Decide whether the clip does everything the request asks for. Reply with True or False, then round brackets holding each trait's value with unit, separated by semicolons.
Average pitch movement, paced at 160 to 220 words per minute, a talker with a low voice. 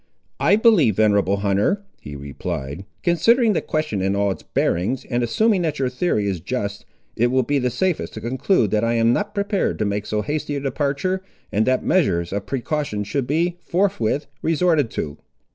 False (8.6 semitones; 185 wpm; 125 Hz)